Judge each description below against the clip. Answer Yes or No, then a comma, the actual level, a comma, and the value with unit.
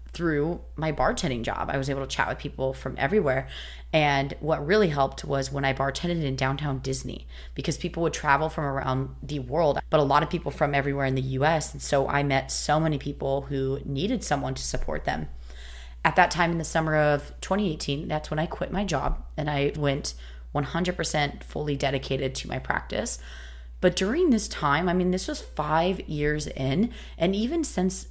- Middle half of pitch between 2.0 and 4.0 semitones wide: Yes, average, 3.5 semitones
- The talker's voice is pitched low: No, medium, 145 Hz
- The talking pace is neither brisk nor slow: Yes, average, 195 wpm